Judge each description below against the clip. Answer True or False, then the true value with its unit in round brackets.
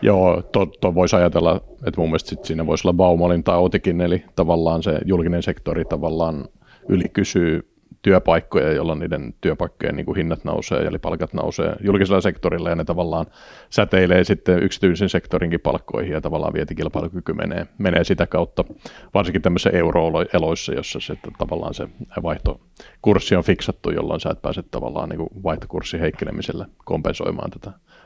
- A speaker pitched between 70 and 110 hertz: True (90 Hz)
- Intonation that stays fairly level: True (2.0 semitones)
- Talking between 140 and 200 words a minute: True (150 wpm)